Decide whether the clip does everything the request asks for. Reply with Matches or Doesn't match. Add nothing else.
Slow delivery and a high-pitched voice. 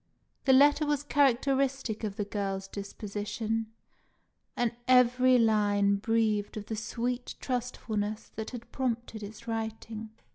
Matches